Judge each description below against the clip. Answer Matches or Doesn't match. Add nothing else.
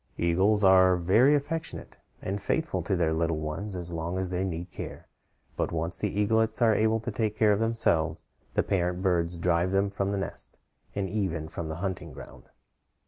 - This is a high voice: Doesn't match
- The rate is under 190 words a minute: Doesn't match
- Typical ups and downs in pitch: Matches